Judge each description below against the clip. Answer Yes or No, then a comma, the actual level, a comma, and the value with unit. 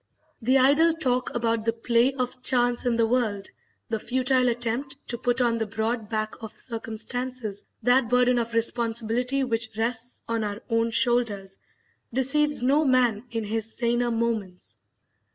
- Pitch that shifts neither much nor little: No, narrow, 1.9 semitones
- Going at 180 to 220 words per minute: No, average, 155 wpm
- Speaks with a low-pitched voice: No, high, 235 Hz